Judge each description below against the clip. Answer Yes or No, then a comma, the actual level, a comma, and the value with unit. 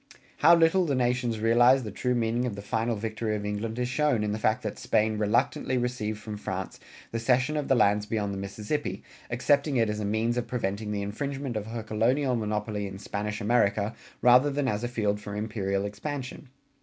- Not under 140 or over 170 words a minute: No, fast, 205 wpm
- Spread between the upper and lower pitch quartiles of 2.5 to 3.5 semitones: Yes, average, 3.1 semitones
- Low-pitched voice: Yes, low, 115 Hz